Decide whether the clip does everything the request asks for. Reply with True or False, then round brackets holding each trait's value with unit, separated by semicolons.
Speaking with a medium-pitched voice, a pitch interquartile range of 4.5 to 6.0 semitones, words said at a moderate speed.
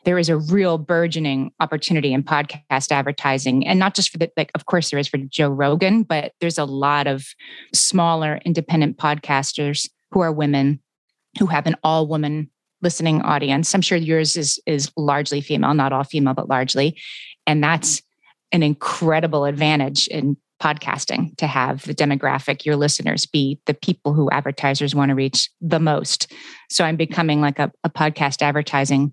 False (150 Hz; 2.5 semitones; 170 wpm)